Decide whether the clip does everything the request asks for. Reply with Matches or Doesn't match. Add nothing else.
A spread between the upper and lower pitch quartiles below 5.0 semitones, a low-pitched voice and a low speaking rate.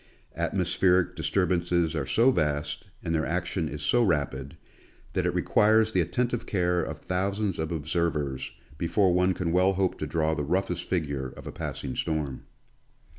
Doesn't match